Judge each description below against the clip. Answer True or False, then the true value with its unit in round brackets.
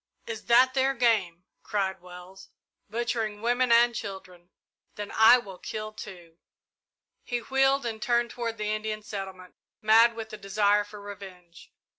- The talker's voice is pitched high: True (215 Hz)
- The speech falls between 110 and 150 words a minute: True (145 wpm)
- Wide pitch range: False (3.6 semitones)